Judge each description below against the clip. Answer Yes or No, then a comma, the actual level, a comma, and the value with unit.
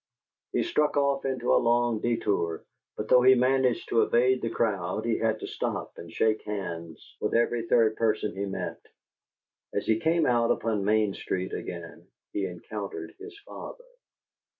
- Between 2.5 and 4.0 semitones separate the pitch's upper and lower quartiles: Yes, average, 3.6 semitones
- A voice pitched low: Yes, low, 115 Hz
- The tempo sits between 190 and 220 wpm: No, average, 165 wpm